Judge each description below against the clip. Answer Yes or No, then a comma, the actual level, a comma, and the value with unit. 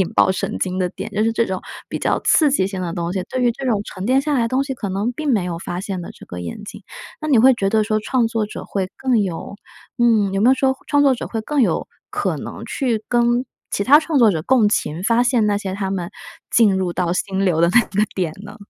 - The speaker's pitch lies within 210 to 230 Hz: Yes, high, 215 Hz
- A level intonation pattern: No, average, 4.5 semitones